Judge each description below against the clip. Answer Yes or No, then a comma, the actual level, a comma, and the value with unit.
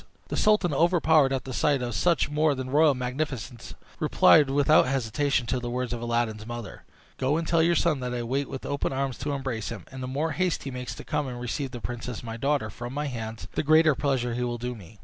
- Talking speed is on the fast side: Yes, fast, 235 wpm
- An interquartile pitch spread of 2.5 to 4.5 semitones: Yes, average, 3.6 semitones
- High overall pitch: No, low, 130 Hz